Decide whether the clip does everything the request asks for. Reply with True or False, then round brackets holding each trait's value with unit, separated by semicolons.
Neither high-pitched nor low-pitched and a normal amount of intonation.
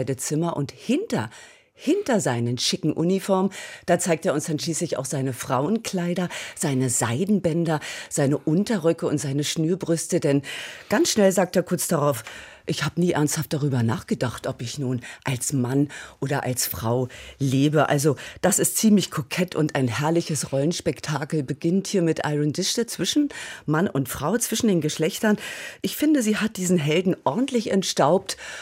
True (160 Hz; 4.8 semitones)